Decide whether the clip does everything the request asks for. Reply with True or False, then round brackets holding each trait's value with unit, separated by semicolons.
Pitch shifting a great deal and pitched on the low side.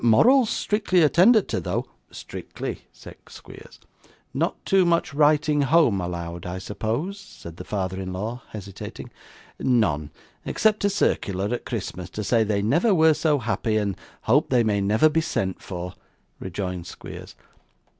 True (9.0 semitones; 110 Hz)